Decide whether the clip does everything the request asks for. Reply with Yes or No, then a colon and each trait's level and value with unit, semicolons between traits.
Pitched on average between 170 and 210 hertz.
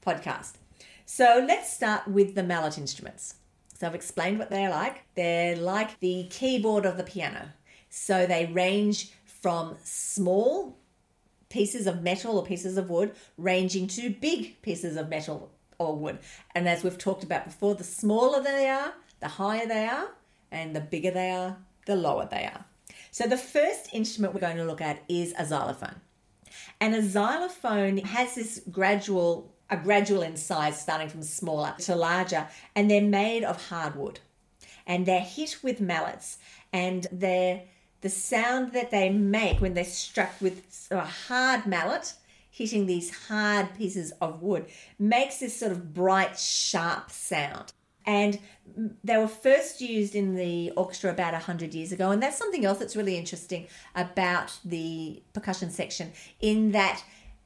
Yes: high, 190 Hz